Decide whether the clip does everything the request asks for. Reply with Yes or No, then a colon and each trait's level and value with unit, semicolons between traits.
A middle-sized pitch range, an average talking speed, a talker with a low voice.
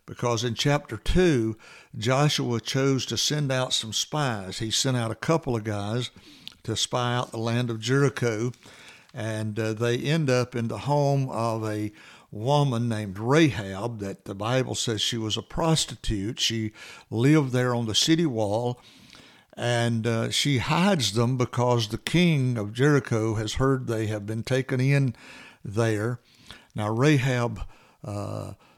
Yes: average, 3.2 semitones; average, 155 wpm; low, 120 Hz